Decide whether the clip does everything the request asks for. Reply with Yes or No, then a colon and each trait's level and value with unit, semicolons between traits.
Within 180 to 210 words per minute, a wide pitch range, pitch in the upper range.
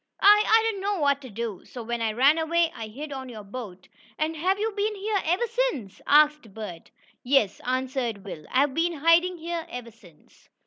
Yes: average, 195 wpm; wide, 7.2 semitones; very high, 280 Hz